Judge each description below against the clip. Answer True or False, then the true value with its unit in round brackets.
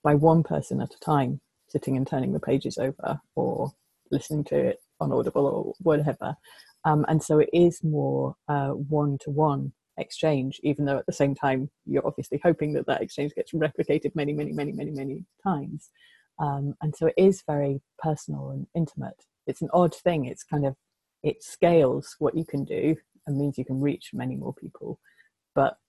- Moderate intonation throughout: False (2.2 semitones)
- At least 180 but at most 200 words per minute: True (195 wpm)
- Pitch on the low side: False (150 Hz)